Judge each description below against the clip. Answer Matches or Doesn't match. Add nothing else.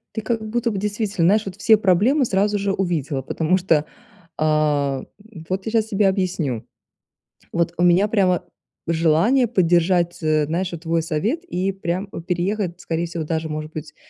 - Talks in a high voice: Doesn't match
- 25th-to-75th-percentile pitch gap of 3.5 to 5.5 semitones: Matches